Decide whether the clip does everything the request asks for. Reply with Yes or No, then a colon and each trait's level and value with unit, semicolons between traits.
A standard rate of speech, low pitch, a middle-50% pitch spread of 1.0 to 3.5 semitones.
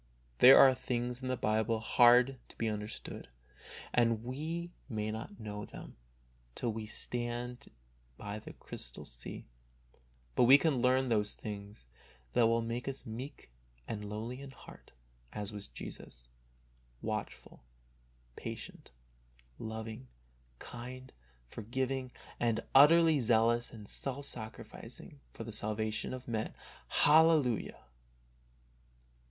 No: slow, 120 wpm; low, 120 Hz; average, 3.0 semitones